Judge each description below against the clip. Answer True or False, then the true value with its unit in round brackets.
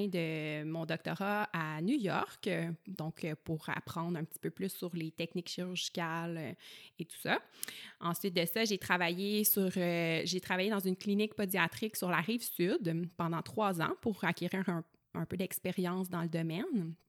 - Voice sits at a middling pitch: True (175 Hz)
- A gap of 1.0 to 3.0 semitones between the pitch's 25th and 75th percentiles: True (2.7 semitones)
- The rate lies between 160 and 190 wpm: True (170 wpm)